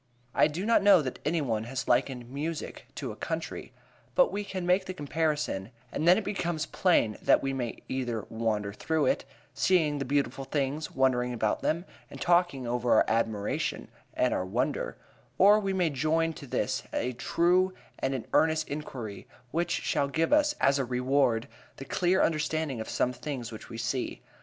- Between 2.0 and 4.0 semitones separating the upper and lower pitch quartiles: No, wide, 5.5 semitones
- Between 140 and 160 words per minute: No, average, 180 wpm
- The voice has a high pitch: No, medium, 140 Hz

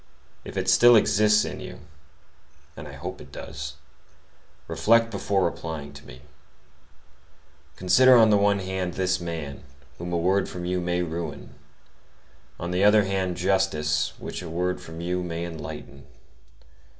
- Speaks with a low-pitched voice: Yes, very low, 90 Hz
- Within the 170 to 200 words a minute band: No, average, 140 wpm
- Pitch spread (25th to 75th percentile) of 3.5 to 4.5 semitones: No, average, 2.9 semitones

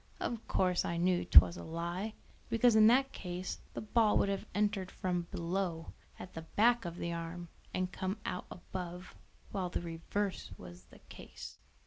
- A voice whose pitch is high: No, medium, 180 Hz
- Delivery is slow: No, average, 170 wpm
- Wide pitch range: No, average, 3.3 semitones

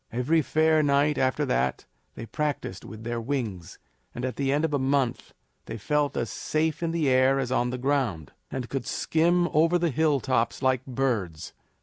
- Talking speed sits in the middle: Yes, average, 185 wpm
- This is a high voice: No, low, 135 Hz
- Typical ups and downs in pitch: Yes, average, 3.7 semitones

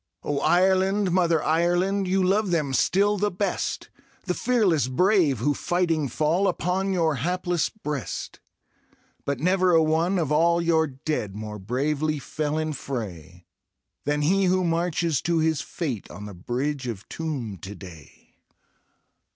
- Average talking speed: Yes, average, 145 wpm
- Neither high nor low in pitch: Yes, medium, 160 Hz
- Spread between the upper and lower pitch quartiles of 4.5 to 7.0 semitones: Yes, average, 4.8 semitones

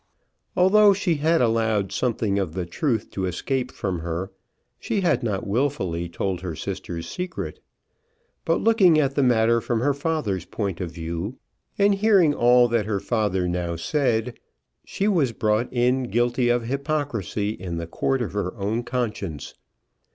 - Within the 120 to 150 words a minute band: No, average, 160 wpm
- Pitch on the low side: Yes, low, 115 Hz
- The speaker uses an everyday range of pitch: No, wide, 6.5 semitones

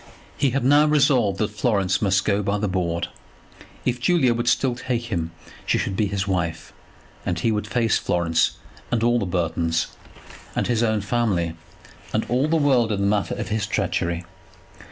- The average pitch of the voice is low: Yes, low, 105 Hz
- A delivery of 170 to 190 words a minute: Yes, average, 180 wpm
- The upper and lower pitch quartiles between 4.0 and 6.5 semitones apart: Yes, average, 4.5 semitones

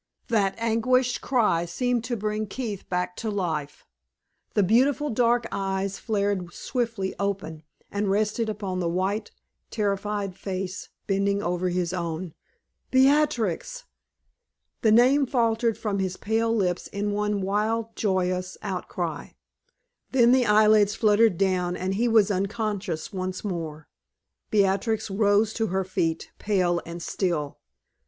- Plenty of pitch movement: No, average, 3.4 semitones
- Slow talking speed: Yes, slow, 130 wpm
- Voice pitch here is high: Yes, high, 200 Hz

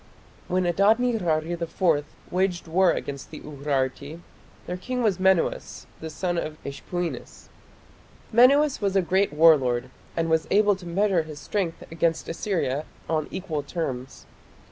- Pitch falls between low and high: Yes, medium, 170 Hz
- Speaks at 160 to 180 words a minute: No, average, 145 wpm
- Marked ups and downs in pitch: No, average, 3.9 semitones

